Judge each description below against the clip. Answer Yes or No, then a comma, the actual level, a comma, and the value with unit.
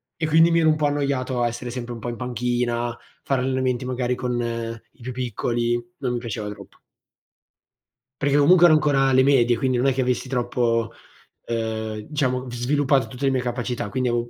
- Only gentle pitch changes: Yes, narrow, 2.2 semitones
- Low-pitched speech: Yes, low, 125 Hz